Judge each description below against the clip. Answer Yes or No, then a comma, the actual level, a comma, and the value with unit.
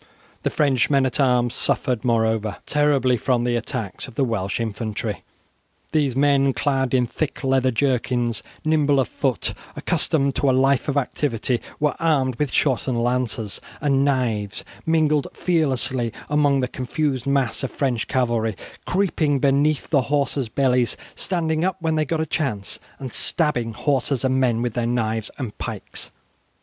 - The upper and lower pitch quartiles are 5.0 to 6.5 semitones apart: No, average, 3.3 semitones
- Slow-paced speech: No, average, 155 wpm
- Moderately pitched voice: No, low, 130 Hz